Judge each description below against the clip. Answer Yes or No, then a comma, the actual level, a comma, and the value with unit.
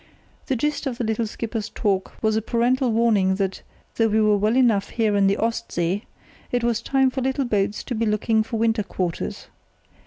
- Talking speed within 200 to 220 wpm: Yes, fast, 205 wpm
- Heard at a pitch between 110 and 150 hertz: No, high, 225 Hz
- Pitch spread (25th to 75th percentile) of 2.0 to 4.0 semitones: Yes, narrow, 2.5 semitones